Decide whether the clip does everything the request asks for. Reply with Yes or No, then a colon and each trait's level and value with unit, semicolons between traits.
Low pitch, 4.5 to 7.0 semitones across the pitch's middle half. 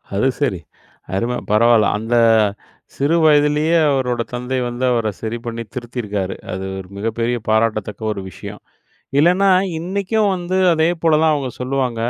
Yes: low, 125 Hz; average, 5.2 semitones